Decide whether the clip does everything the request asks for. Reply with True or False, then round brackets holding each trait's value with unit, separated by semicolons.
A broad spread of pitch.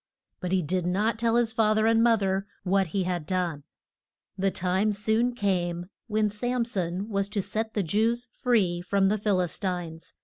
False (3.4 semitones)